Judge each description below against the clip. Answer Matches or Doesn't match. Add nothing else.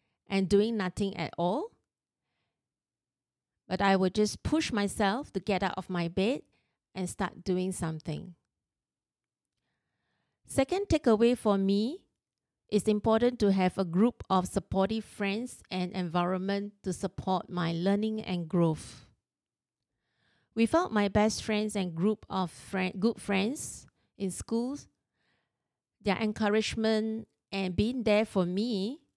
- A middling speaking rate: Doesn't match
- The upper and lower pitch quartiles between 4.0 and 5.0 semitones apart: Doesn't match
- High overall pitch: Matches